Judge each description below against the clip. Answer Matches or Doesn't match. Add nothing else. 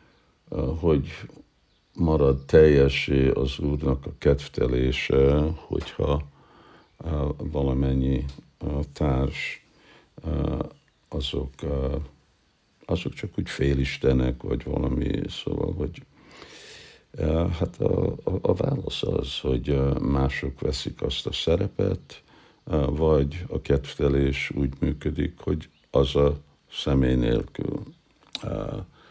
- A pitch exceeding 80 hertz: Doesn't match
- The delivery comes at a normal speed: Doesn't match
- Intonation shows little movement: Matches